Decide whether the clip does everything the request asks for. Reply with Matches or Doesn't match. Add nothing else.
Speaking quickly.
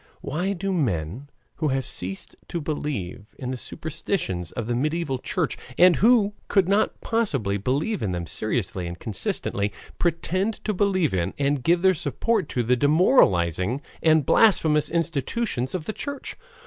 Doesn't match